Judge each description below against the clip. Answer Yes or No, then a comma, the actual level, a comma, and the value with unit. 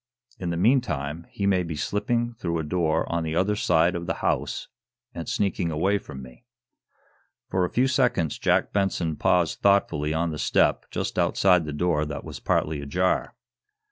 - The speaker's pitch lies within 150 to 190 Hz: No, very low, 85 Hz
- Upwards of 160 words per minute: Yes, average, 175 wpm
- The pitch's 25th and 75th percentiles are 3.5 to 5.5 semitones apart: Yes, average, 4.0 semitones